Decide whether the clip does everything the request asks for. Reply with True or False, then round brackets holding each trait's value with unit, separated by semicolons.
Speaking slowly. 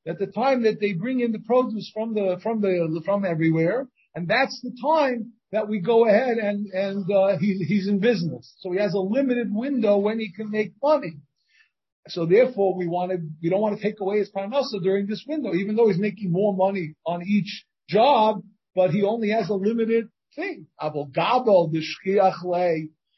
False (195 wpm)